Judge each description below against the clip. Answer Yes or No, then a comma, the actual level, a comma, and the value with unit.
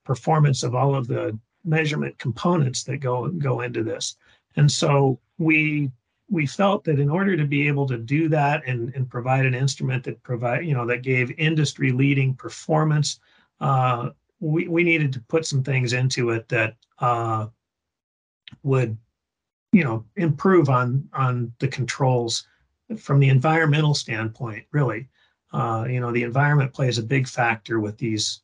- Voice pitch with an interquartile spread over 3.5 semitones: Yes, average, 3.9 semitones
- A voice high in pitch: No, low, 135 Hz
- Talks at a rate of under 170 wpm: Yes, average, 160 wpm